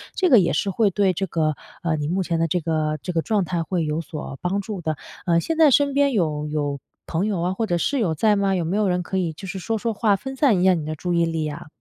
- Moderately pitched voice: Yes, medium, 180 Hz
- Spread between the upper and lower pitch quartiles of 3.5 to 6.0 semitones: Yes, average, 4.3 semitones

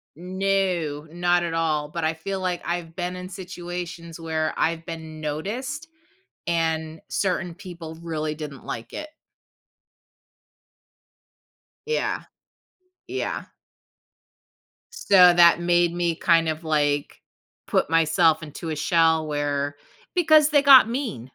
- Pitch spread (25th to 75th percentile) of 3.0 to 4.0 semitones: No, narrow, 2.5 semitones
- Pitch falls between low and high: Yes, medium, 170 Hz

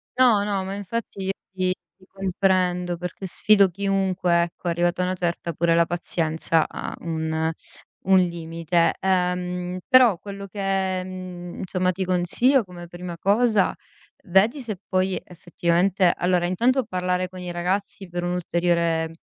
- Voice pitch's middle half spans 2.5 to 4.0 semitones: No, narrow, 1.9 semitones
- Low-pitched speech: No, medium, 180 Hz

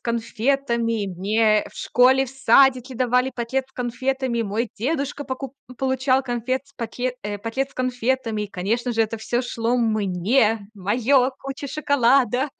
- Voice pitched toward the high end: Yes, high, 245 Hz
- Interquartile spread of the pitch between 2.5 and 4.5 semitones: Yes, average, 2.8 semitones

